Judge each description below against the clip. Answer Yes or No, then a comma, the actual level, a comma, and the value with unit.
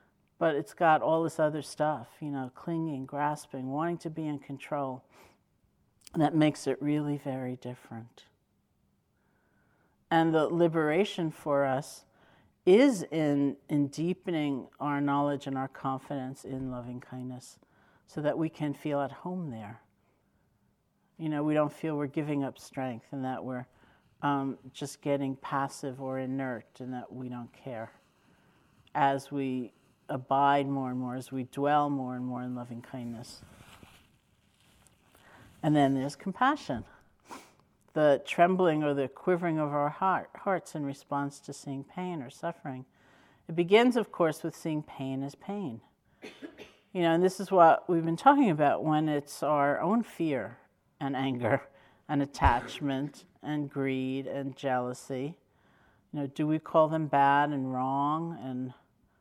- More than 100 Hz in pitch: Yes, medium, 140 Hz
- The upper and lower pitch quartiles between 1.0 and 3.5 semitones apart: Yes, average, 3.0 semitones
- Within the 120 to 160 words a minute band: Yes, average, 150 wpm